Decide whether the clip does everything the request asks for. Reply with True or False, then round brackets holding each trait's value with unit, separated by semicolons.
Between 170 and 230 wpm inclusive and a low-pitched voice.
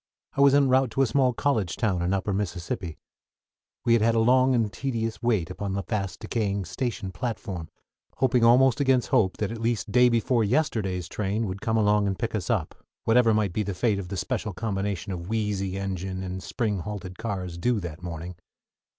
True (200 wpm; 105 Hz)